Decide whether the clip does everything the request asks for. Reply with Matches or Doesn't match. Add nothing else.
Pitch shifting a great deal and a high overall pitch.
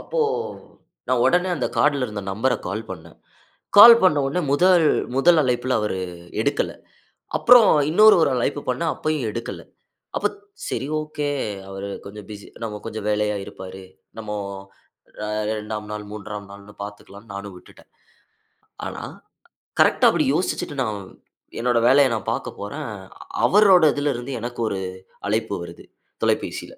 Doesn't match